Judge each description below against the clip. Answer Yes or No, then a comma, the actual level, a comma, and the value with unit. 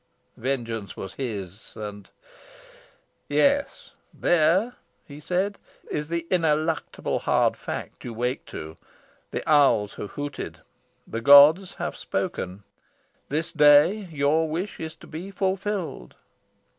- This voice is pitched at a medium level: Yes, medium, 150 Hz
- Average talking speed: No, slow, 115 wpm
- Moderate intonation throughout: No, wide, 6.7 semitones